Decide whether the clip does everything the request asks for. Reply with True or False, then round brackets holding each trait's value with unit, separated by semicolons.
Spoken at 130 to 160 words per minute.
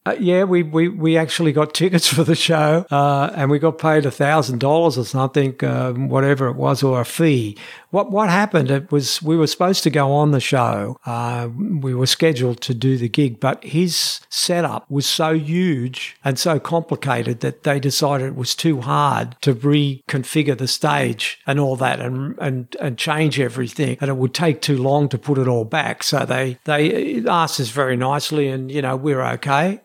False (200 wpm)